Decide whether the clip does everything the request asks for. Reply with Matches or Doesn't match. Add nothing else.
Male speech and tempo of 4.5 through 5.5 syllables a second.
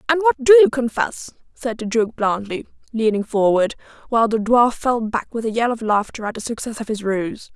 Doesn't match